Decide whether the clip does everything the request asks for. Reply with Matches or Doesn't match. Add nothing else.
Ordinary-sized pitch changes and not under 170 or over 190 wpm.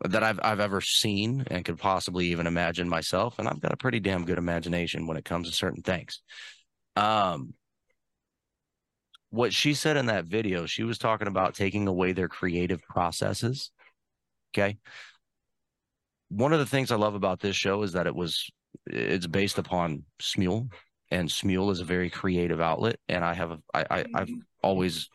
Matches